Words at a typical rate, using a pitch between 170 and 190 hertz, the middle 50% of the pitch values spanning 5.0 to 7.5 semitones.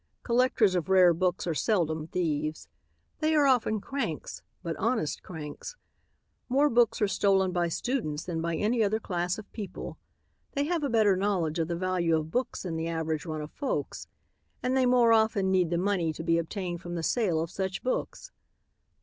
Yes: average, 185 wpm; medium, 185 Hz; wide, 5.5 semitones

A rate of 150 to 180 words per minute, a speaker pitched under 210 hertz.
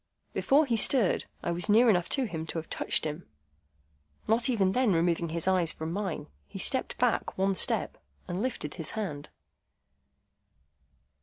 Yes: average, 160 wpm; medium, 185 Hz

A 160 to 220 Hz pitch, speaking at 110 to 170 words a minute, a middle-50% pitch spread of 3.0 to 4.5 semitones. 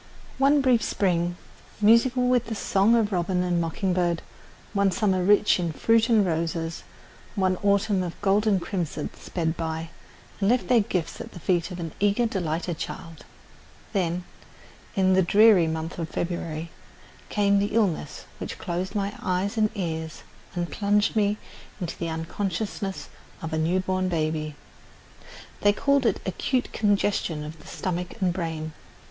Yes: medium, 185 Hz; average, 155 wpm; average, 3.6 semitones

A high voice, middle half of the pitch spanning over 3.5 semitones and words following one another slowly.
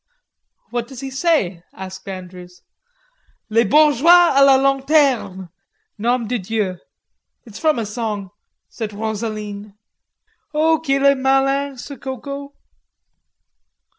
Yes: high, 245 Hz; average, 5.1 semitones; slow, 110 wpm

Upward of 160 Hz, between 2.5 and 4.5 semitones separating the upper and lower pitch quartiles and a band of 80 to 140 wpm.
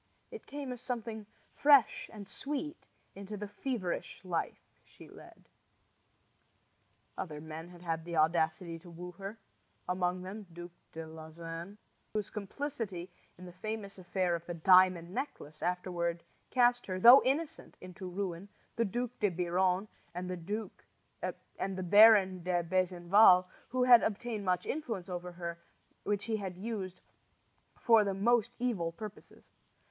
Yes: medium, 185 Hz; average, 4.0 semitones; slow, 135 wpm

